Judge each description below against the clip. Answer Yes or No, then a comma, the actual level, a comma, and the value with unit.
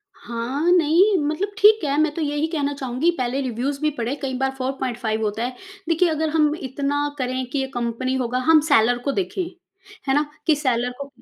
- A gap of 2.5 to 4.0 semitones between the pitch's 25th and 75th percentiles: Yes, average, 3.5 semitones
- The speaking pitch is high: Yes, very high, 275 Hz